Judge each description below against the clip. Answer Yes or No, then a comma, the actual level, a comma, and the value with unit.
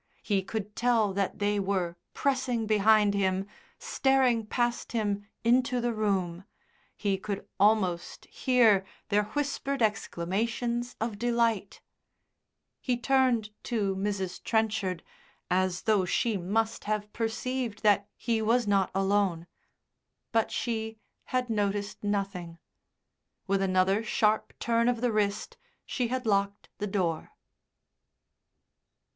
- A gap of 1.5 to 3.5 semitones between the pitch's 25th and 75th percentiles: Yes, average, 3.0 semitones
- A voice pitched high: Yes, high, 210 Hz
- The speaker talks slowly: Yes, slow, 115 wpm